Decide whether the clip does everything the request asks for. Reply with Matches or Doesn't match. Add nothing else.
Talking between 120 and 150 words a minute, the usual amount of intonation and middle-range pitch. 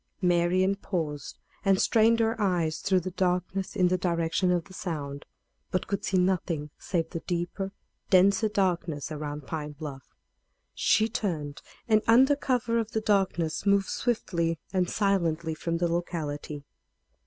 Matches